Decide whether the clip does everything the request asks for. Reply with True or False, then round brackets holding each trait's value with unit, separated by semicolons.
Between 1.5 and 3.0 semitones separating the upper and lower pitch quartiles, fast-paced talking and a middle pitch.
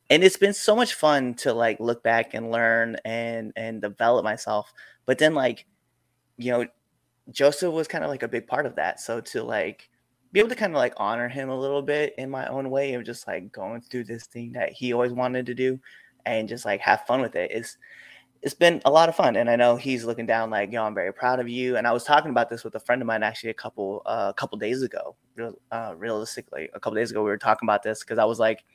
False (2.7 semitones; 260 wpm; 120 Hz)